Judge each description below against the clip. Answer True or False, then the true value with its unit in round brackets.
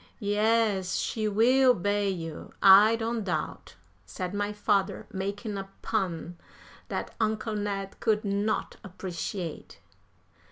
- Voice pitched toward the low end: False (205 Hz)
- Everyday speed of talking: False (115 wpm)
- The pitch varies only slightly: True (2.2 semitones)